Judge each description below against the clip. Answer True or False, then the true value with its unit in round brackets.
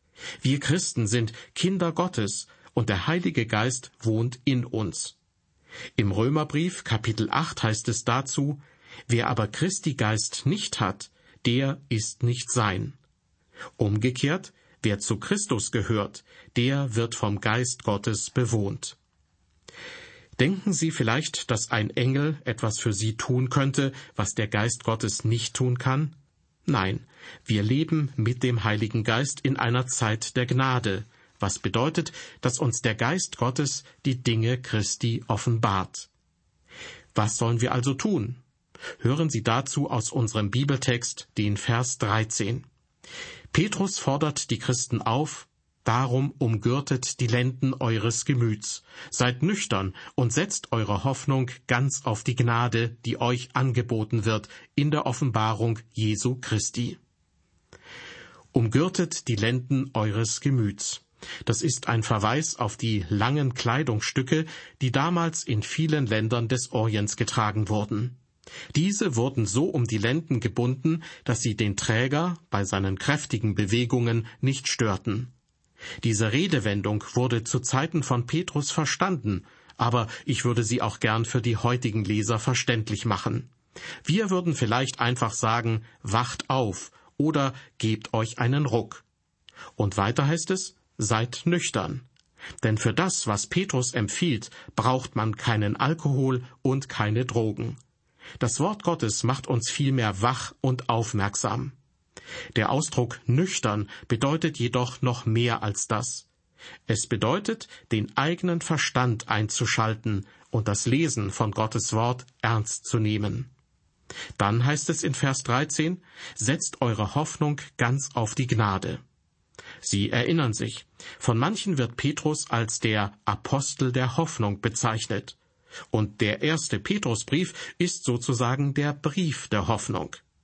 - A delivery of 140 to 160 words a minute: False (130 wpm)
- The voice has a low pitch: True (120 Hz)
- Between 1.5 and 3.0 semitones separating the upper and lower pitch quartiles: False (3.6 semitones)